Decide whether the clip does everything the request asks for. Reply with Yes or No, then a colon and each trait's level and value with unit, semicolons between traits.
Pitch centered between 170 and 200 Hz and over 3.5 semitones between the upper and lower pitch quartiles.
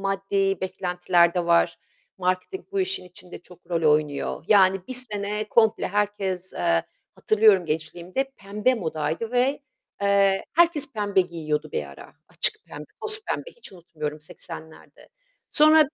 Yes: high, 190 Hz; average, 4.2 semitones